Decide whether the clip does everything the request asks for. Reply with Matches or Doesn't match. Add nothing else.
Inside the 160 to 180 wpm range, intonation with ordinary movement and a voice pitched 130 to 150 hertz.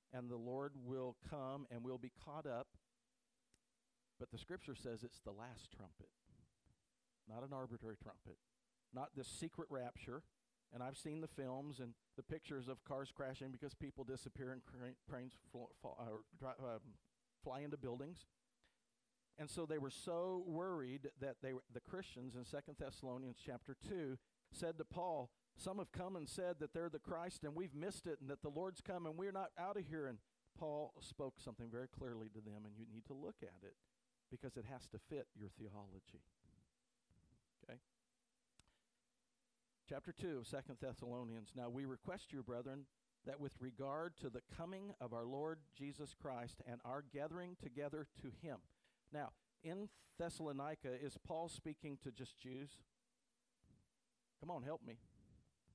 Matches